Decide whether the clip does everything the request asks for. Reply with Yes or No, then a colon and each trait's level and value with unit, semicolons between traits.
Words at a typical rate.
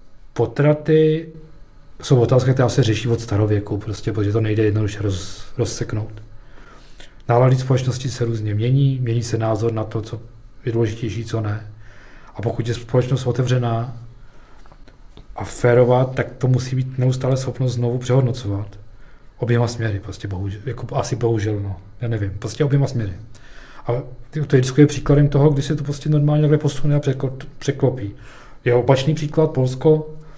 Yes: average, 150 wpm